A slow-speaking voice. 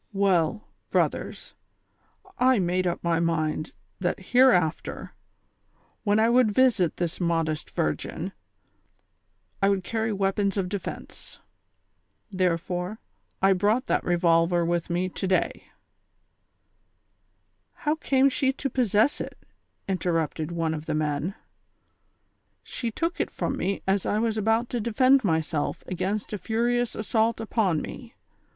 Yes: slow, 130 wpm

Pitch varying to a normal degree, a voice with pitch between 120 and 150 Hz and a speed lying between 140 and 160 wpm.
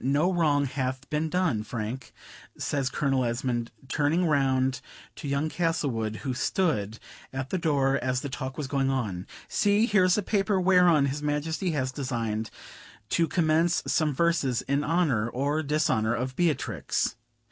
Yes: average, 4.0 semitones; medium, 140 Hz; average, 155 wpm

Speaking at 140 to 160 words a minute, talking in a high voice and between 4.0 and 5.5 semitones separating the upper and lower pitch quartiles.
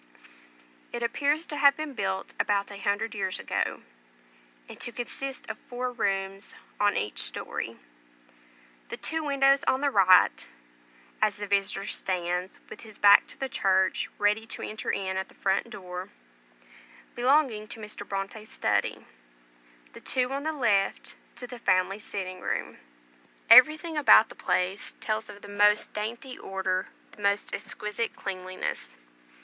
Yes: average, 150 wpm; high, 210 Hz; average, 4.4 semitones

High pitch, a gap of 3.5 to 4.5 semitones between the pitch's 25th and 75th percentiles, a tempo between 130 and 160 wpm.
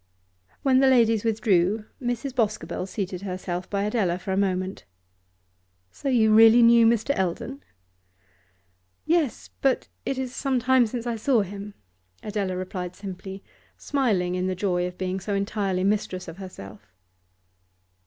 Yes: high, 205 Hz; average, 4.2 semitones; average, 145 wpm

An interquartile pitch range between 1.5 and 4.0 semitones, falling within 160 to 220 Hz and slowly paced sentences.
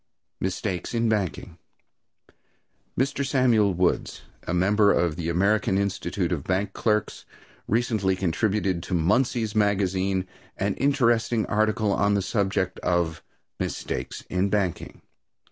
No: average, 2.9 semitones; low, 100 Hz; slow, 115 wpm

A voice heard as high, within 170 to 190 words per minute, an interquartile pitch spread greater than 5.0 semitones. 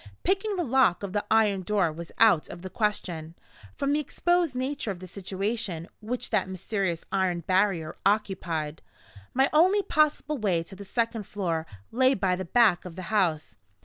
Yes: high, 200 Hz; average, 175 wpm; wide, 5.6 semitones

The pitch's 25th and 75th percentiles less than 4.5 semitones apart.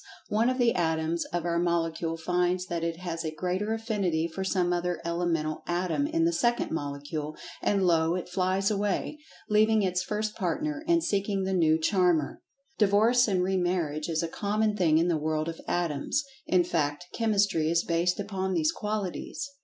Yes: average, 4.0 semitones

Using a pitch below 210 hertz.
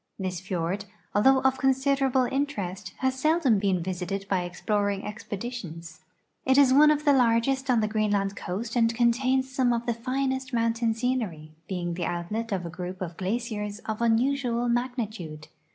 No: high, 230 Hz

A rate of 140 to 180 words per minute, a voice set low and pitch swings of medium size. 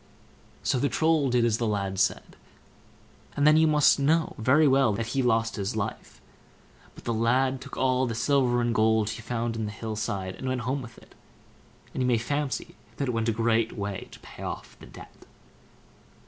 No: fast, 205 wpm; low, 120 Hz; average, 3.2 semitones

